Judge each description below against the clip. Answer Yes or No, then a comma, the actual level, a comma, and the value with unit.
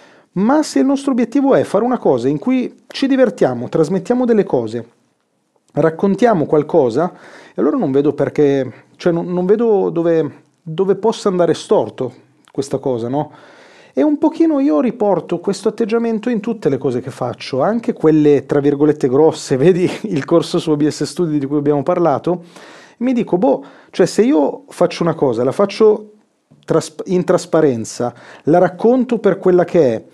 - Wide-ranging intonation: Yes, wide, 7.4 semitones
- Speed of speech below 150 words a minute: No, average, 160 wpm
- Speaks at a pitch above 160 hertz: Yes, medium, 180 Hz